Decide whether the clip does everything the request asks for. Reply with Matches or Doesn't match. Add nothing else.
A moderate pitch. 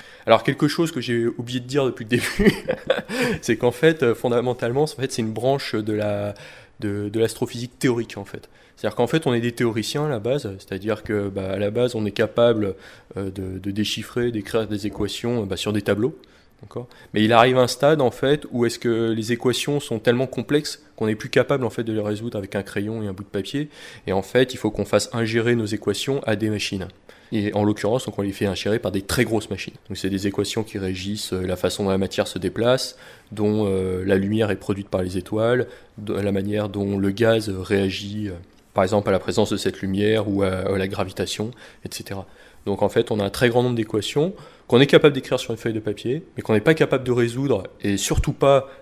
Doesn't match